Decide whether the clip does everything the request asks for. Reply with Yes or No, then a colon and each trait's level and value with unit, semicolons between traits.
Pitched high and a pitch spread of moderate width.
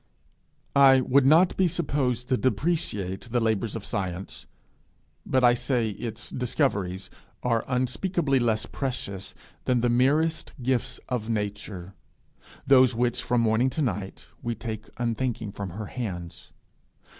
No: low, 120 Hz; average, 3.7 semitones